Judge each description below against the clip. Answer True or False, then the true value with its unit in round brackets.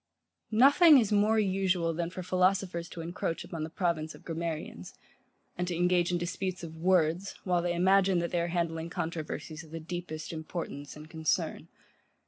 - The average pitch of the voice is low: False (175 Hz)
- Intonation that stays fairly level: True (2.2 semitones)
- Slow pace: False (170 wpm)